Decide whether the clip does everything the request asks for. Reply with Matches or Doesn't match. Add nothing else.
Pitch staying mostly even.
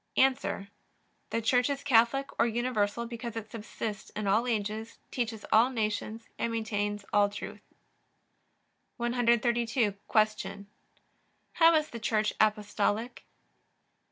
Matches